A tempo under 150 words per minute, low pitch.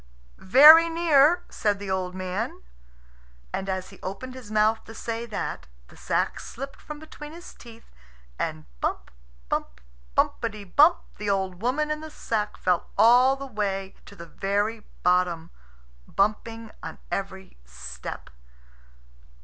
No: average, 140 wpm; high, 215 Hz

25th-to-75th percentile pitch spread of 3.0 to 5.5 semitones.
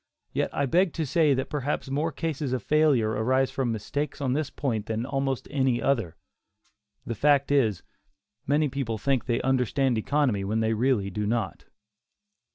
Yes: average, 4.2 semitones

